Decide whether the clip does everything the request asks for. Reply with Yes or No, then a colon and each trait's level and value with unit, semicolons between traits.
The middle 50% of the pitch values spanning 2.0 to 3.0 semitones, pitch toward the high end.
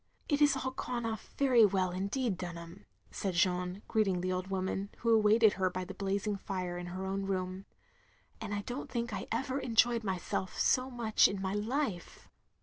No: average, 3.9 semitones; high, 200 Hz